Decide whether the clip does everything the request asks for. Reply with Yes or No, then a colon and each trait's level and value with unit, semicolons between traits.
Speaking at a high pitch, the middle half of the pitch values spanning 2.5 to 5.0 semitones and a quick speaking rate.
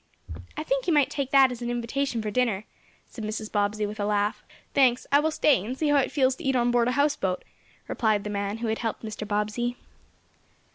Yes: high, 240 Hz; average, 4.2 semitones; fast, 225 wpm